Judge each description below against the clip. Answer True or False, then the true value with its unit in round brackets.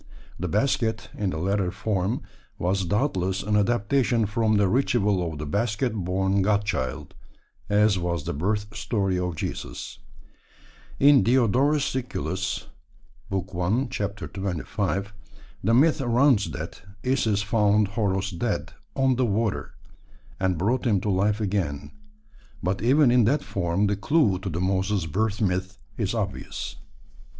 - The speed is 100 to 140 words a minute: True (135 wpm)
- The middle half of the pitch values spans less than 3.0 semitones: False (3.4 semitones)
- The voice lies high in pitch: False (100 Hz)